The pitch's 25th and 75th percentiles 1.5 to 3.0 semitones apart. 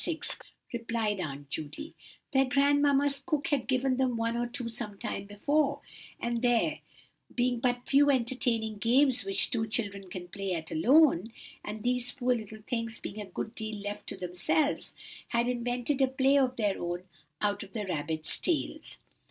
No: average, 4.4 semitones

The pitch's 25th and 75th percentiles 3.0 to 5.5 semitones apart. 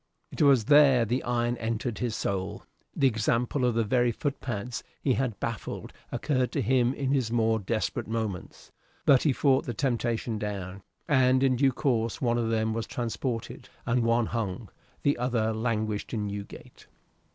No: narrow, 2.6 semitones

